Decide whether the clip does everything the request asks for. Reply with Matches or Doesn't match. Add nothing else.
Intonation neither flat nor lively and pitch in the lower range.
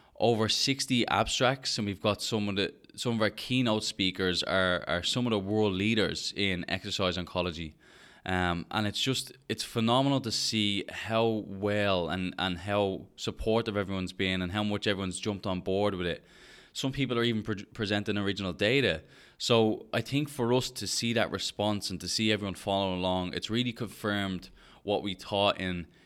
Matches